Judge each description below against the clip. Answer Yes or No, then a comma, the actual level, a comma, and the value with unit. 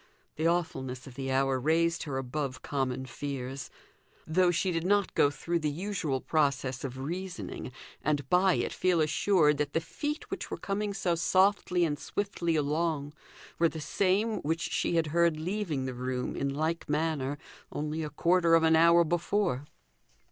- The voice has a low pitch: No, medium, 160 Hz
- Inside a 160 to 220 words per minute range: Yes, average, 170 wpm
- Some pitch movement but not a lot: Yes, average, 3.9 semitones